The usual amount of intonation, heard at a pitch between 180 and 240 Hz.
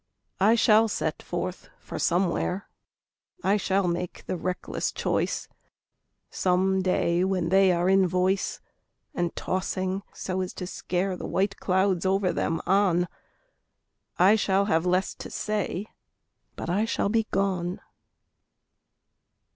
No: narrow, 1.5 semitones; medium, 185 Hz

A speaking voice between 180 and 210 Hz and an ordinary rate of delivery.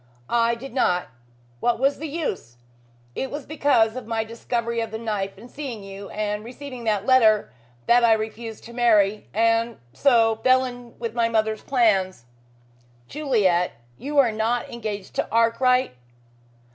No: high, 230 Hz; average, 155 wpm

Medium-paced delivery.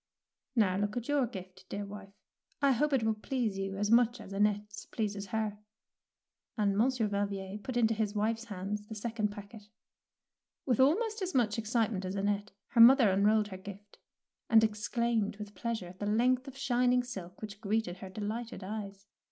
Yes: average, 175 wpm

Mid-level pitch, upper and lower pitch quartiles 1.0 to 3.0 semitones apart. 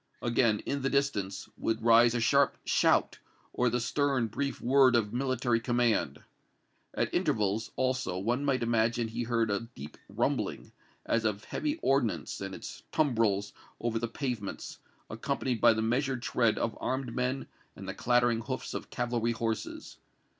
No: low, 120 Hz; narrow, 2.4 semitones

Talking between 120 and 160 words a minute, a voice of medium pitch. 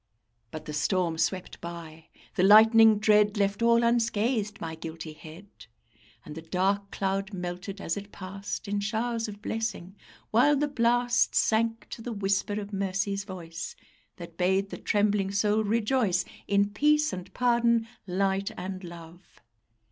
No: average, 150 wpm; high, 200 Hz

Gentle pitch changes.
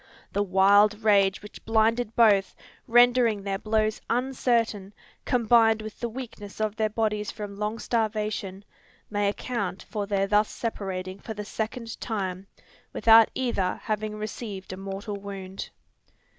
Yes: narrow, 2.1 semitones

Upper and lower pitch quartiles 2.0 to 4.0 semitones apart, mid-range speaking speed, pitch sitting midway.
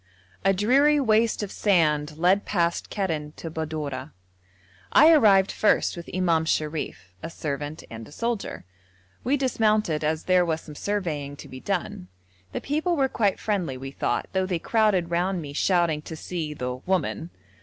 No: average, 5.3 semitones; average, 165 wpm; medium, 175 Hz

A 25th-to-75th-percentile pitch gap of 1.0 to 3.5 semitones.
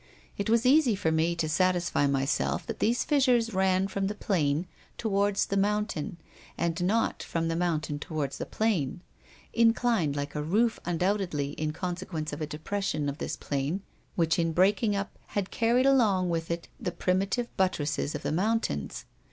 No: average, 4.8 semitones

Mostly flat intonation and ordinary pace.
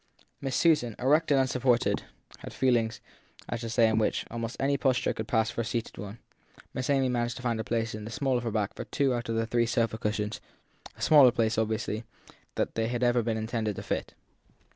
No: narrow, 2.2 semitones; fast, 230 wpm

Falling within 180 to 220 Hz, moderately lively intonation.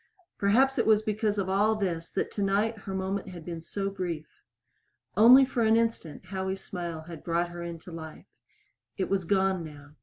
Yes: high, 190 Hz; average, 3.5 semitones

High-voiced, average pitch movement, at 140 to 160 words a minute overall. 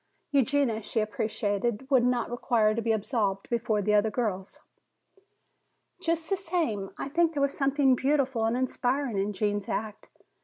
Yes: high, 235 Hz; average, 4.5 semitones; average, 155 wpm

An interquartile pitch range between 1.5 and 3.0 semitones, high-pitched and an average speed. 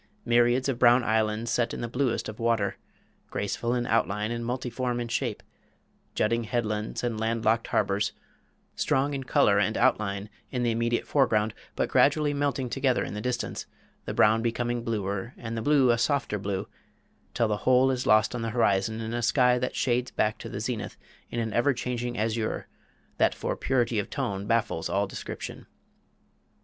No: narrow, 2.4 semitones; low, 115 Hz; average, 180 wpm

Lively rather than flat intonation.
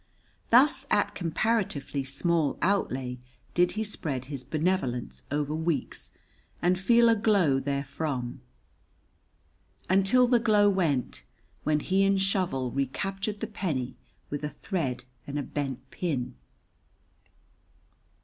Yes: wide, 6.2 semitones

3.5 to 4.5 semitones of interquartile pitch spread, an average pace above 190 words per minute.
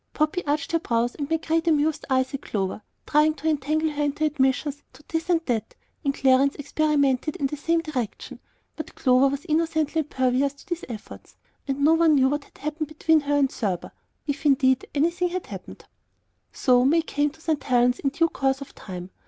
No: average, 2.9 semitones; average, 200 wpm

